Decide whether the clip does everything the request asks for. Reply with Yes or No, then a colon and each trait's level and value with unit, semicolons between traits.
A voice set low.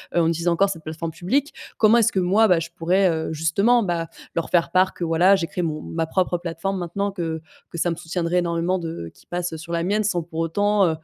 No: medium, 175 Hz